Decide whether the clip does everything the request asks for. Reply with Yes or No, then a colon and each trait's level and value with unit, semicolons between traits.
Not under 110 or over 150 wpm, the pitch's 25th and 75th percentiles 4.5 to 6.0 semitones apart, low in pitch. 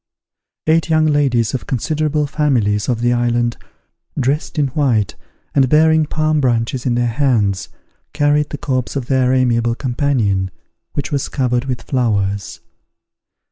No: average, 140 wpm; average, 3.8 semitones; low, 130 Hz